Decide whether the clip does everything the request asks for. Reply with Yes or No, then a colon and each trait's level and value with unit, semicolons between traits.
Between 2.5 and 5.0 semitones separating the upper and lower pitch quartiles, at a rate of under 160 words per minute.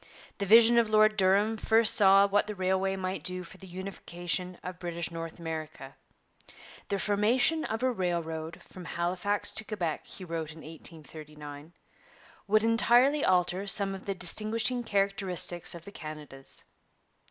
Yes: average, 3.8 semitones; average, 150 wpm